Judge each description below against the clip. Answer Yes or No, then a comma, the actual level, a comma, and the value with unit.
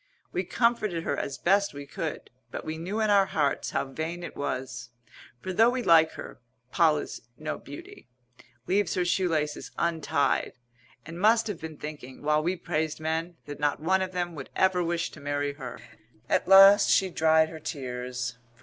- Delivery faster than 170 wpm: Yes, average, 185 wpm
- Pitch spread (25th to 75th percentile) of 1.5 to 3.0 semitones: No, average, 4.3 semitones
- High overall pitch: No, medium, 160 Hz